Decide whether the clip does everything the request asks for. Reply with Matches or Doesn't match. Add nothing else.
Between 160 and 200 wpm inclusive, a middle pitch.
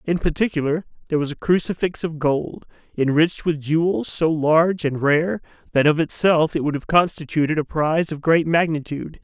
Matches